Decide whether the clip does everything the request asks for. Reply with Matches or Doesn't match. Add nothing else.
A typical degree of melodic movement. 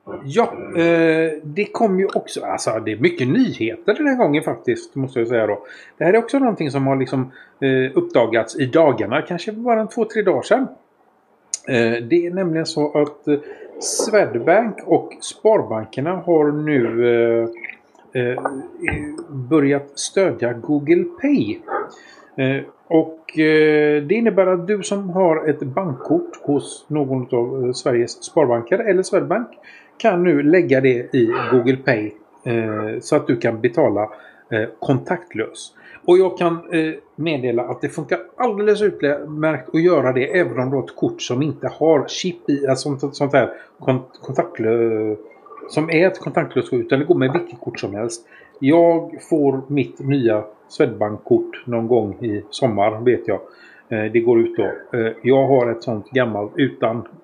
Doesn't match